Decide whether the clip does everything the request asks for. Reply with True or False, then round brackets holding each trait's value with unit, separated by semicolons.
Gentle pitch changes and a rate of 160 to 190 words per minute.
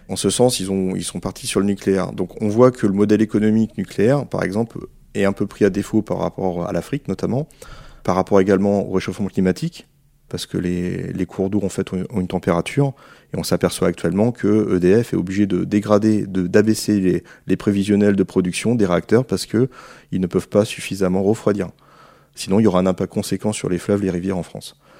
False (2.2 semitones; 220 wpm)